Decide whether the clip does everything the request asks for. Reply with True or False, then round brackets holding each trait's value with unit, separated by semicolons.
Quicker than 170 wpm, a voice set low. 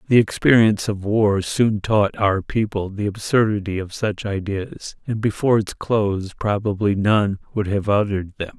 False (160 wpm; 105 Hz)